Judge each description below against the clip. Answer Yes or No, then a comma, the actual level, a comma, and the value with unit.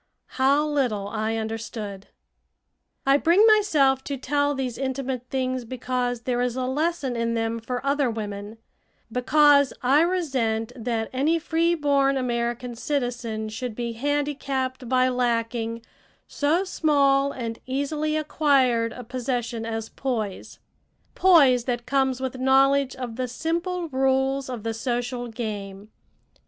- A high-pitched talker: Yes, very high, 255 Hz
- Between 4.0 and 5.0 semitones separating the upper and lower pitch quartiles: No, average, 3.3 semitones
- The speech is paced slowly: Yes, slow, 130 wpm